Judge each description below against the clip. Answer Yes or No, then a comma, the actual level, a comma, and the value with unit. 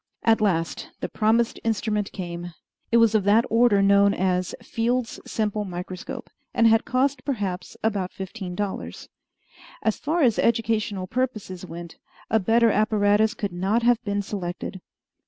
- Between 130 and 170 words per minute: Yes, average, 145 wpm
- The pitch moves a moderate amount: Yes, average, 3.3 semitones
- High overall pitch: Yes, high, 210 Hz